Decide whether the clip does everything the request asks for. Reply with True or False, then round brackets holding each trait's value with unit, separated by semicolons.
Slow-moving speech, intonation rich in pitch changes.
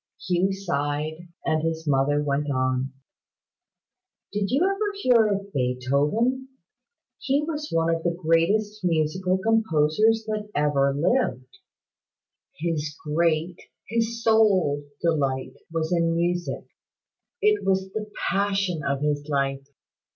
True (115 wpm; 6.2 semitones)